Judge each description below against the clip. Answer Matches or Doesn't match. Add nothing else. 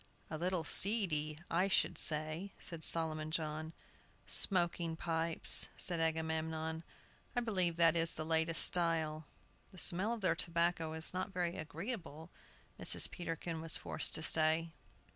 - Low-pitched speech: Doesn't match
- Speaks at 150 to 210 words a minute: Doesn't match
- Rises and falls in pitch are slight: Matches